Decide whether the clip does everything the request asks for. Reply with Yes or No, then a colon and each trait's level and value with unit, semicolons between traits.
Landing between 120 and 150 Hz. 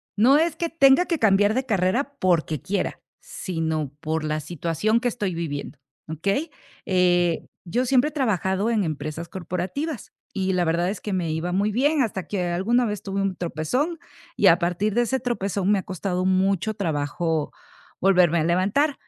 No: high, 190 Hz